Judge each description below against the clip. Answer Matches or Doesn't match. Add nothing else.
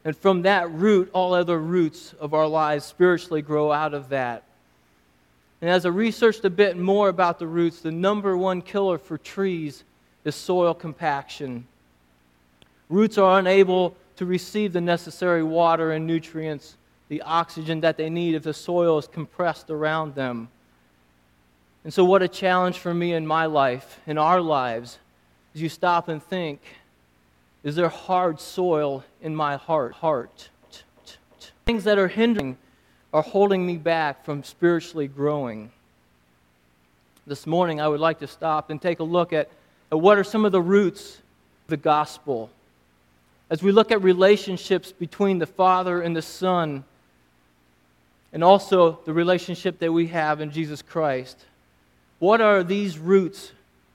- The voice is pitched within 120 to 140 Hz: Doesn't match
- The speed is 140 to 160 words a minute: Matches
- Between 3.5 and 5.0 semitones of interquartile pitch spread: Doesn't match